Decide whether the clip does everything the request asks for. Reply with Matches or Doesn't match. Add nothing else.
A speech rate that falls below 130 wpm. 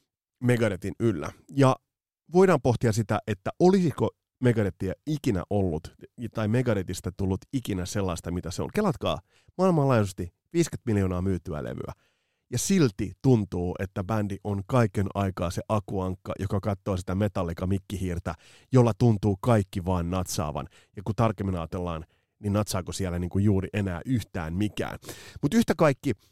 Doesn't match